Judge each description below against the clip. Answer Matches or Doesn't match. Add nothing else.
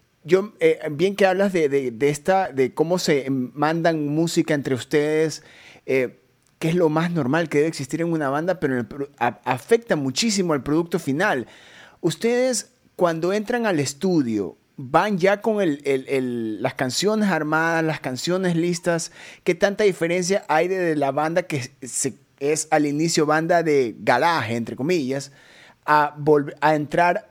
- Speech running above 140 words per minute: Matches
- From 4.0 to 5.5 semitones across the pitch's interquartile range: Matches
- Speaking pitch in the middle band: Matches